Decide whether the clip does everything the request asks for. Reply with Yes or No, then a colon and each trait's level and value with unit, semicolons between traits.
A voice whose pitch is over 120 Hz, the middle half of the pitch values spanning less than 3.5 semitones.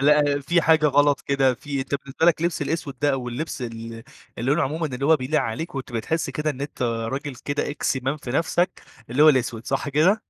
Yes: medium, 140 Hz; average, 3.0 semitones